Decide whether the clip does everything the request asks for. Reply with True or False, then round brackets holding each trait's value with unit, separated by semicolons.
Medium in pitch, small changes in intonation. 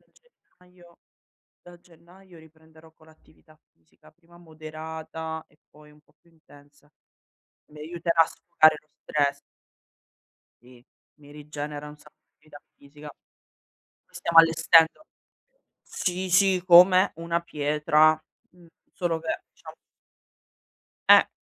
True (160 Hz; 2.2 semitones)